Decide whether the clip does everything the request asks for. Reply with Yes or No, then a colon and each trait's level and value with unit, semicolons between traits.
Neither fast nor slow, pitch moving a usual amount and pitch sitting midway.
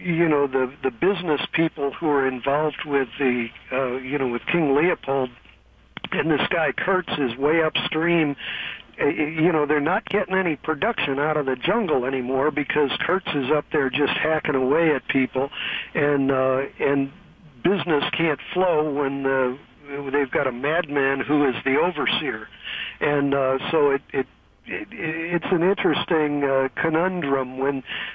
Yes: average, 160 wpm; average, 3.0 semitones; medium, 145 Hz